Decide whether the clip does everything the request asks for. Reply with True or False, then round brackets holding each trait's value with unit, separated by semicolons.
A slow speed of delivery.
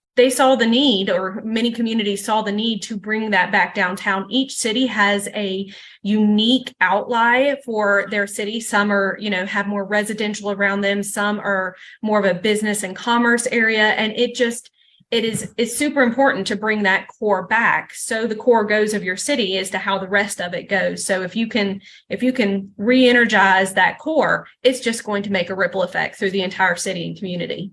False (205 wpm)